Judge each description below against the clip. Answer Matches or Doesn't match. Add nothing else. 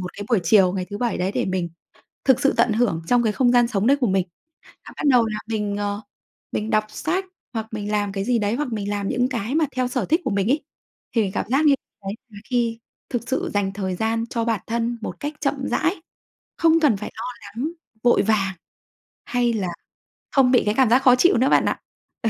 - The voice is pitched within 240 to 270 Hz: Doesn't match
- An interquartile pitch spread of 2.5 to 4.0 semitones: Matches